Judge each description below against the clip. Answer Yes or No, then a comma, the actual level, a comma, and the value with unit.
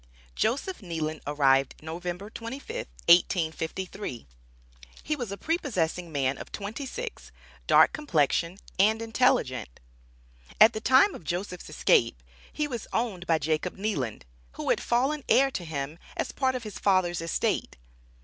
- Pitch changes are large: Yes, wide, 6.9 semitones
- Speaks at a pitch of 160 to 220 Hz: Yes, medium, 185 Hz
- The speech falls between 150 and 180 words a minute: No, average, 140 wpm